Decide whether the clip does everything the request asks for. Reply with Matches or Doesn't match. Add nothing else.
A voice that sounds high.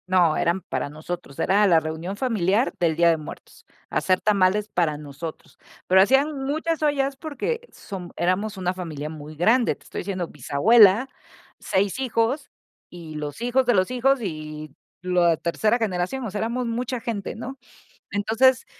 Matches